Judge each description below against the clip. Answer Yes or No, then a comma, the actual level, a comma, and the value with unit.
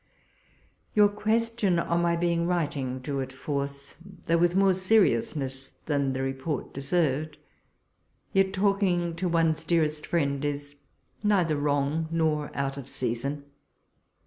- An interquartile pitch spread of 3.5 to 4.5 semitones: Yes, average, 4.0 semitones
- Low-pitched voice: No, medium, 155 Hz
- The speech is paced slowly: Yes, slow, 130 wpm